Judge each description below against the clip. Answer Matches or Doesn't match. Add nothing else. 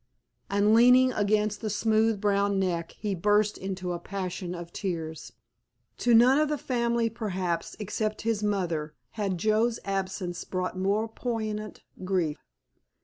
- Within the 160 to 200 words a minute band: Doesn't match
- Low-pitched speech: Doesn't match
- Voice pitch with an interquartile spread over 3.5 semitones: Doesn't match